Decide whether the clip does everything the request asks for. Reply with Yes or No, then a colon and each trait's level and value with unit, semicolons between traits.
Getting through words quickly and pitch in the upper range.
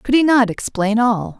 Yes: fast, 215 wpm; high, 230 Hz